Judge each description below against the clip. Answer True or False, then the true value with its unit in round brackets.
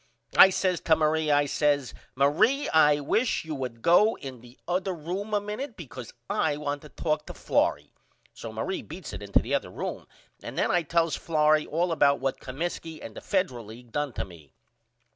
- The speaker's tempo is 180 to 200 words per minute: True (195 wpm)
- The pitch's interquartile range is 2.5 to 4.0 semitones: False (4.5 semitones)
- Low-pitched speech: False (150 Hz)